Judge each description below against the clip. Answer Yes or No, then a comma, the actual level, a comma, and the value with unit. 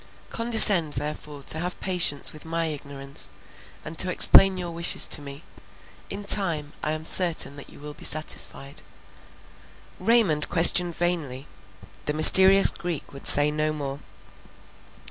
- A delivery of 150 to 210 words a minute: No, average, 140 wpm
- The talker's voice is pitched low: No, medium, 155 Hz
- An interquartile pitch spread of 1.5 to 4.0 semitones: Yes, average, 3.3 semitones